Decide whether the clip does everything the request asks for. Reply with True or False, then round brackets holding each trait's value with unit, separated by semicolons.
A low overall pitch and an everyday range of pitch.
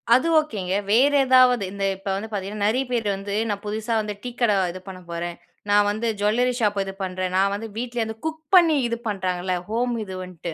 False (210 Hz; 3.7 semitones)